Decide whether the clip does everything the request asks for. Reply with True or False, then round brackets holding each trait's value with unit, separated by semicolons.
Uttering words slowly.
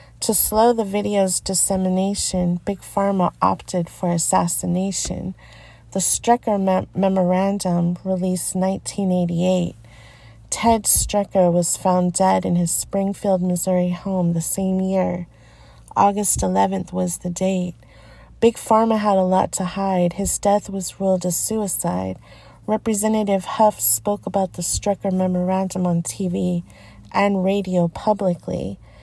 True (120 wpm)